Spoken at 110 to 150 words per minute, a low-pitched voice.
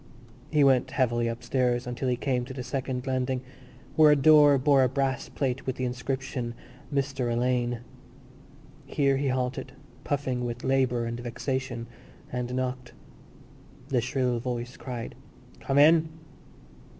Yes: average, 140 wpm; low, 130 Hz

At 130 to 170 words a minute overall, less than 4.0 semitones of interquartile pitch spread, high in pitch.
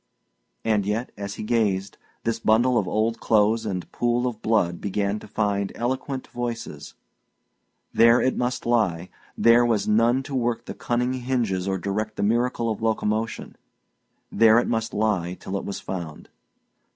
No: average, 160 wpm; average, 2.9 semitones; low, 110 Hz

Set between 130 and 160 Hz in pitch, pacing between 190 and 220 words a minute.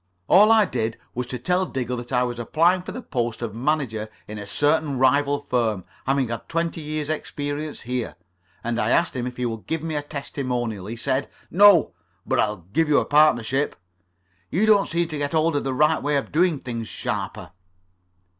Yes: medium, 140 Hz; average, 200 wpm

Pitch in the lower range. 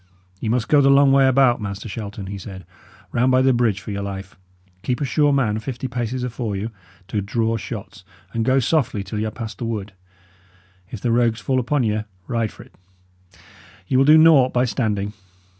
Yes: low, 115 Hz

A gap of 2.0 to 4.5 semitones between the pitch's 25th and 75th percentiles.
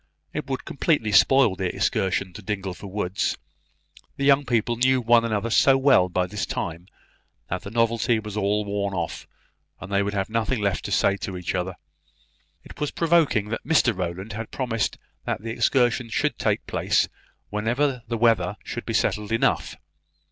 Yes: average, 3.5 semitones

